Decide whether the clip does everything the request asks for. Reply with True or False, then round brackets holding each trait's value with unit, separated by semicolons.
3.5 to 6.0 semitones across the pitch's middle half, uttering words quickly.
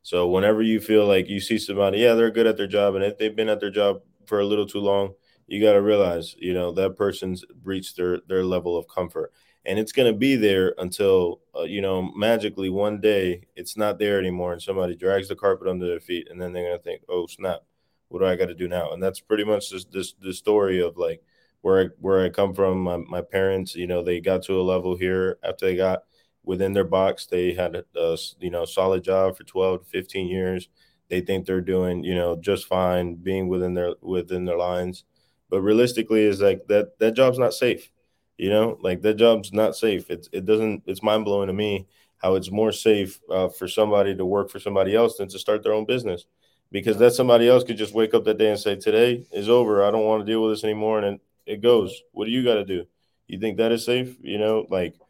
False (2.9 semitones; 240 wpm)